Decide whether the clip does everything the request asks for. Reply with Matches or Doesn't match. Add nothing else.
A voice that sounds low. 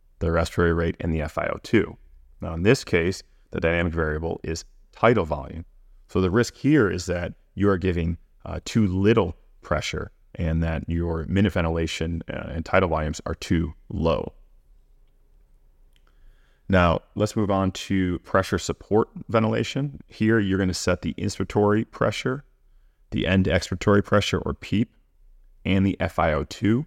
Matches